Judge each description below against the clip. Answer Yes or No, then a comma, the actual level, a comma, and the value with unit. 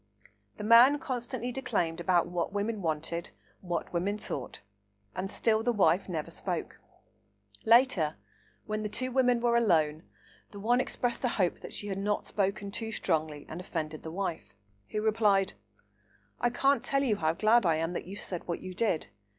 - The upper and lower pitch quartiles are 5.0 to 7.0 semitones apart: Yes, wide, 5.4 semitones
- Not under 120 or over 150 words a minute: No, average, 175 wpm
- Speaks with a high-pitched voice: Yes, high, 200 Hz